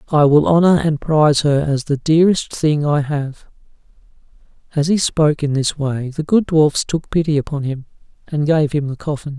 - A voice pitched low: No, medium, 150 Hz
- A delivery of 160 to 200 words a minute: Yes, average, 190 wpm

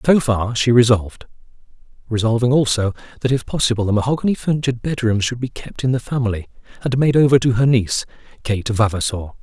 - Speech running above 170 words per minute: No, average, 165 wpm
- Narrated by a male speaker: Yes, male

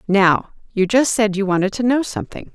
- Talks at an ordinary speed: No, fast, 210 wpm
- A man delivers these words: No, female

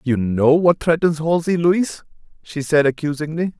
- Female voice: No, male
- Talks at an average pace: Yes, average, 150 wpm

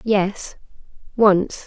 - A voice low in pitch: No, high, 200 Hz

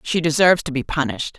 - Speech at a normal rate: No, fast, 215 wpm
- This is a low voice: No, medium, 150 Hz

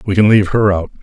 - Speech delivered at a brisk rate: Yes, fast, 295 wpm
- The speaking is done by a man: Yes, male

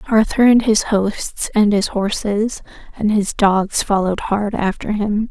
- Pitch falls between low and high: No, high, 210 Hz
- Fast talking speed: No, average, 160 wpm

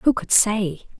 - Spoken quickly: No, average, 180 wpm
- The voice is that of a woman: Yes, female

